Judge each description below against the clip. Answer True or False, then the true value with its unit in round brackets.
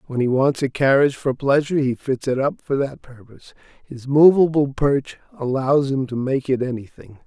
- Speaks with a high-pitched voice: False (135 Hz)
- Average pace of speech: True (190 wpm)